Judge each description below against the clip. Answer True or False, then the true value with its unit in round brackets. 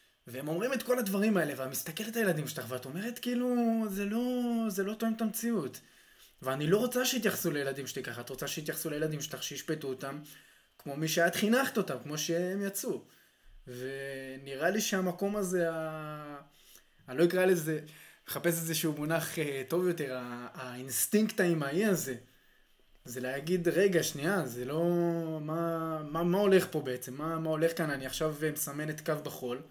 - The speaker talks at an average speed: False (170 wpm)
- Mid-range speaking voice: True (160 Hz)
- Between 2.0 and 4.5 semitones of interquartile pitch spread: False (5.3 semitones)